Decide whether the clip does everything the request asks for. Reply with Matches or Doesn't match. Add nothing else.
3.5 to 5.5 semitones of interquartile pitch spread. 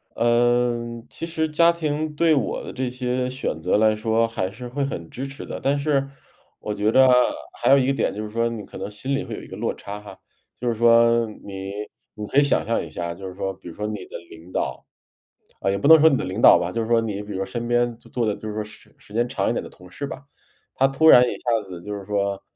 Matches